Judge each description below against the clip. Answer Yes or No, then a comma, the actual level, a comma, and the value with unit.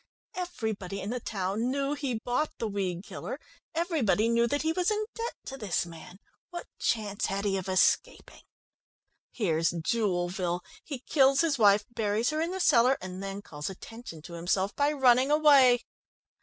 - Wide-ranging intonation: Yes, wide, 6.6 semitones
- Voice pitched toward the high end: Yes, high, 225 Hz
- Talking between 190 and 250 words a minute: No, average, 170 wpm